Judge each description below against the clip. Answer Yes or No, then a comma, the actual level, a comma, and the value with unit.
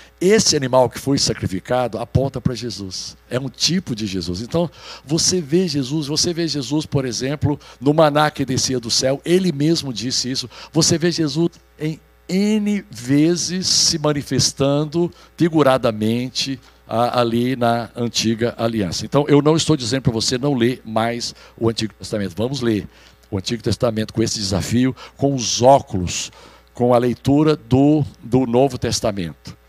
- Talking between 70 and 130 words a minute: No, average, 155 wpm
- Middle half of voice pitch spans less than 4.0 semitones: No, average, 4.6 semitones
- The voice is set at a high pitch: No, low, 130 Hz